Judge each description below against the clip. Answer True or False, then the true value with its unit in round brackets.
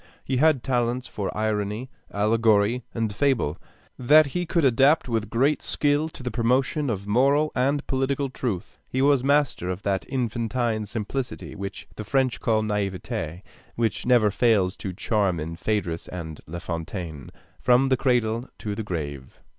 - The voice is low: True (115 Hz)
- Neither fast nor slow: True (155 wpm)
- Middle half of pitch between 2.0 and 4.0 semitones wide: False (4.8 semitones)